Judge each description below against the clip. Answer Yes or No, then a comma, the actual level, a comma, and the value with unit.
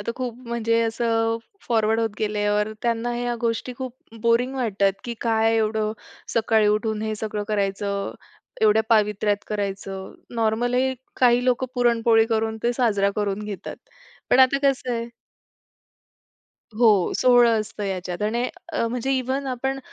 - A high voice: Yes, high, 225 Hz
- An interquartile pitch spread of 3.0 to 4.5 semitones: No, narrow, 2.4 semitones